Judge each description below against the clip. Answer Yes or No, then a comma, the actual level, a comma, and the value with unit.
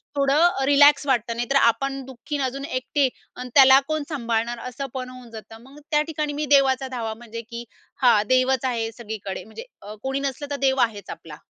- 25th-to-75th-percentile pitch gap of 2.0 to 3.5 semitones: Yes, average, 3.0 semitones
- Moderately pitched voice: No, very high, 260 Hz